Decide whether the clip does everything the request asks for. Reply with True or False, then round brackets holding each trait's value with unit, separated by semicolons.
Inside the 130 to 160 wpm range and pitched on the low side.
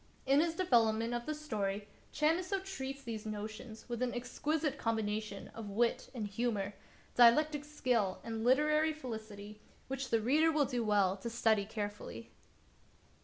False (145 wpm; 235 Hz)